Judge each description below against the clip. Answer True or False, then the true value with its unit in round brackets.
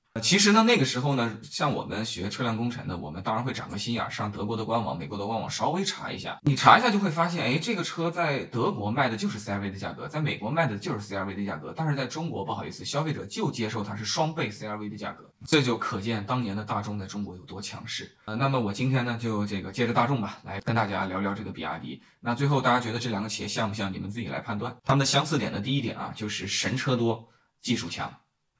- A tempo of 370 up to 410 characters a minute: True (395 characters per minute)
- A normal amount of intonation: True (4.7 semitones)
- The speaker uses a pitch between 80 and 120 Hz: True (115 Hz)